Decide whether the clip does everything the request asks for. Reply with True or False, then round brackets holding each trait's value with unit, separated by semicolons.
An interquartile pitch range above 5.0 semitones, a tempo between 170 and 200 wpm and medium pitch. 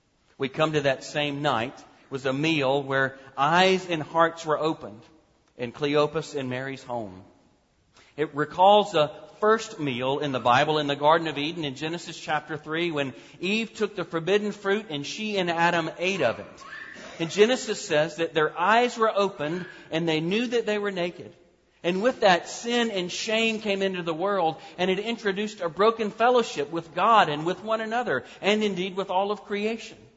True (5.4 semitones; 185 wpm; 170 Hz)